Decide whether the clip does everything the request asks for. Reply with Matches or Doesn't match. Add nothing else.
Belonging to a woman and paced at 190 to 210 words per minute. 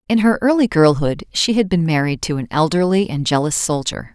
Matches